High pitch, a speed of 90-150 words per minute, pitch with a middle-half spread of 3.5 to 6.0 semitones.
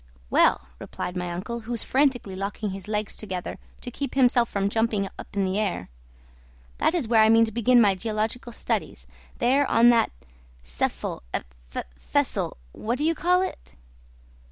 No: high, 225 Hz; average, 165 wpm; average, 3.8 semitones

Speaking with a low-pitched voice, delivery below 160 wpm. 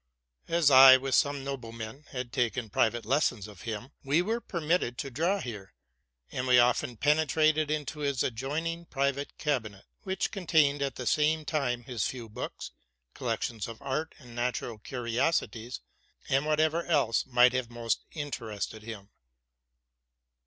Yes: low, 130 Hz; average, 145 wpm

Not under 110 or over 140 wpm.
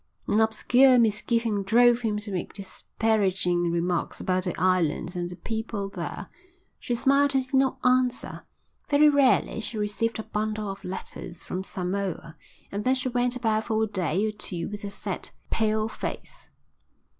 No: average, 165 wpm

